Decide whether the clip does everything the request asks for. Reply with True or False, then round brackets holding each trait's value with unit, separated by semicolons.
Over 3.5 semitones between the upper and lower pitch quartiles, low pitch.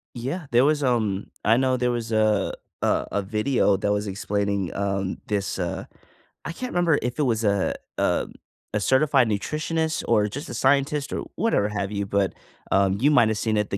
True (5.2 semitones; 110 Hz)